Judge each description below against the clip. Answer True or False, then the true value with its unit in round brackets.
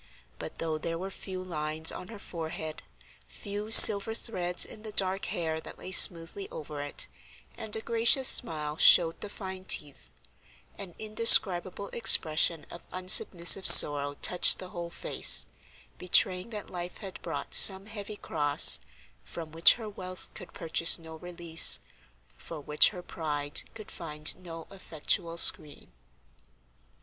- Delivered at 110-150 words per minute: True (140 wpm)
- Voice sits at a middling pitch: True (175 Hz)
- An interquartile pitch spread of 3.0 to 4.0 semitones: True (3.5 semitones)